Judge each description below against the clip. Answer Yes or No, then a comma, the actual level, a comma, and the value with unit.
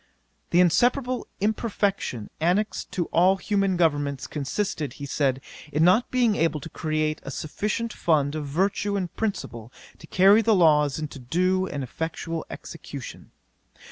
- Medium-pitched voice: Yes, medium, 165 Hz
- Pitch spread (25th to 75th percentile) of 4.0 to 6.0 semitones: Yes, wide, 5.4 semitones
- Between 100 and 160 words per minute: Yes, average, 140 wpm